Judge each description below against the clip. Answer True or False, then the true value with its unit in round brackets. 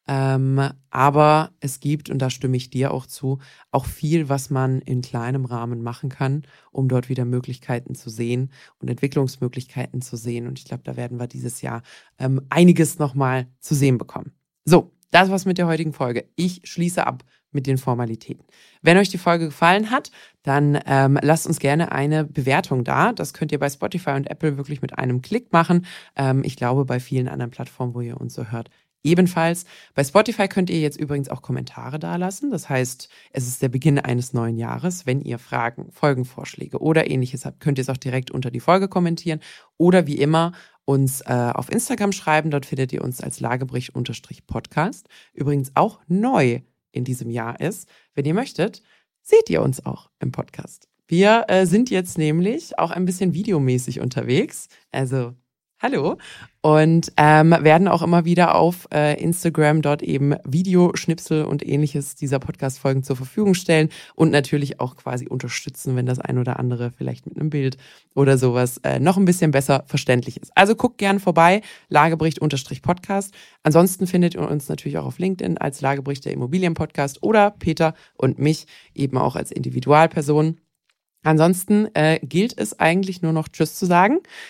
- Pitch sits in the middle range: True (145 Hz)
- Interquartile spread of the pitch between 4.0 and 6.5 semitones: True (4.4 semitones)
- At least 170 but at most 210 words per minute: True (180 wpm)